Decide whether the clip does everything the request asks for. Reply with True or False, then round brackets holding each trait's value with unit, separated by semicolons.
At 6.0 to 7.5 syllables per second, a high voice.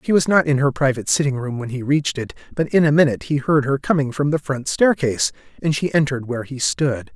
False (6.4 syllables/s; 140 Hz)